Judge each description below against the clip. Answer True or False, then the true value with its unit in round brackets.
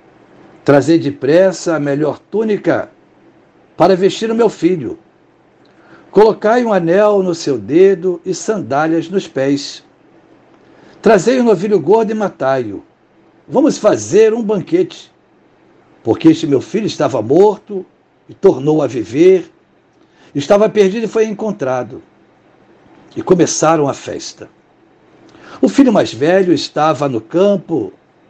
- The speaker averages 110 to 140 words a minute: True (120 wpm)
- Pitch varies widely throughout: False (5.0 semitones)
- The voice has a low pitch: False (195 Hz)